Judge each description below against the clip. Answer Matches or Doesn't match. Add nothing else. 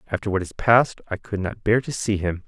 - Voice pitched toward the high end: Doesn't match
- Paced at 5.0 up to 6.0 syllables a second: Matches